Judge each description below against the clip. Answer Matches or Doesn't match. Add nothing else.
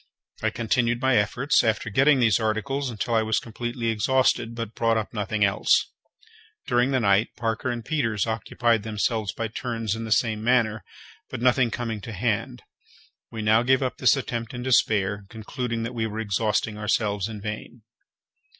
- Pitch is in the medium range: Doesn't match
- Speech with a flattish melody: Matches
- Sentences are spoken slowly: Doesn't match